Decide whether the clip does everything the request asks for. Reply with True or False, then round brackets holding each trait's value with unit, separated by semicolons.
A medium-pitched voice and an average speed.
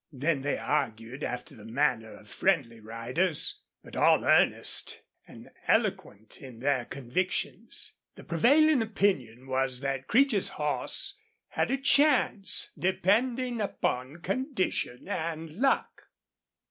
False (155 Hz; 115 wpm)